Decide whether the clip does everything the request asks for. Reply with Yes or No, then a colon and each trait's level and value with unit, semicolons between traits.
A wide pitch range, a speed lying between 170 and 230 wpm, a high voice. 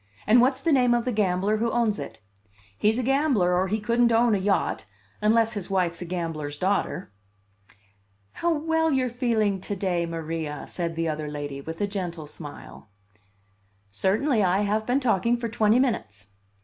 Yes: wide, 5.9 semitones; average, 175 wpm; high, 205 Hz